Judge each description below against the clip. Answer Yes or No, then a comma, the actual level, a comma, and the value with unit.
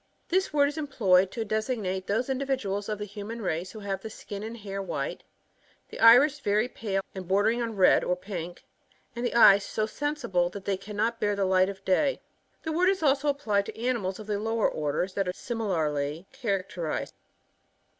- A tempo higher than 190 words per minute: No, average, 185 wpm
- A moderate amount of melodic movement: Yes, average, 4.0 semitones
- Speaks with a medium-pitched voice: No, high, 210 Hz